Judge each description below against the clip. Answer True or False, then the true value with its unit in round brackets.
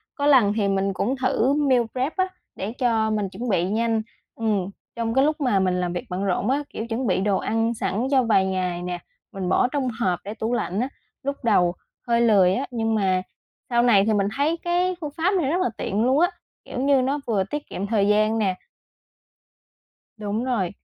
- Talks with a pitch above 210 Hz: True (225 Hz)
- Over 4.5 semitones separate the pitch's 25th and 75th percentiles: True (5.0 semitones)